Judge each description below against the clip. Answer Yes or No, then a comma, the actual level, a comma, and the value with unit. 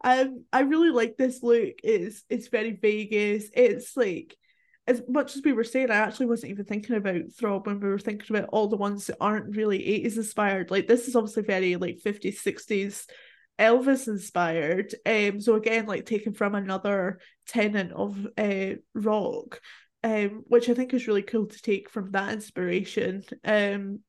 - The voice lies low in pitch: No, high, 215 Hz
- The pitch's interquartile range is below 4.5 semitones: Yes, average, 2.8 semitones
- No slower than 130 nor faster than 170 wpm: No, average, 180 wpm